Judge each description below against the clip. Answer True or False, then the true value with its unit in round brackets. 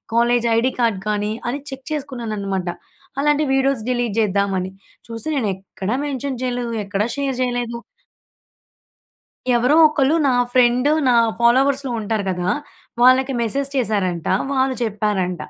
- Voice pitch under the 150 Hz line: False (240 Hz)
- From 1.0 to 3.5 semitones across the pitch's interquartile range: False (4.2 semitones)